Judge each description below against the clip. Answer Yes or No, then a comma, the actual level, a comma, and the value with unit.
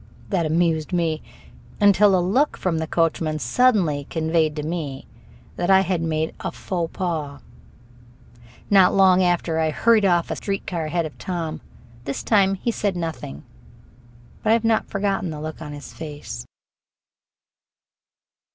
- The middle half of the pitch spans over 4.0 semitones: No, average, 3.6 semitones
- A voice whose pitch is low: No, medium, 170 Hz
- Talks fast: No, average, 150 wpm